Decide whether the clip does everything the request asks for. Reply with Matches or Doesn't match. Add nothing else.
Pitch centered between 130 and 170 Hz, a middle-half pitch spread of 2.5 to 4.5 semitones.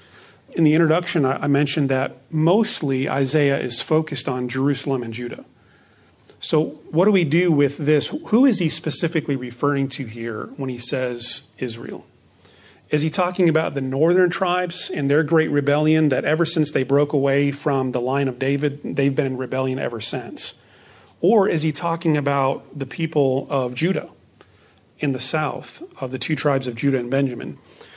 Matches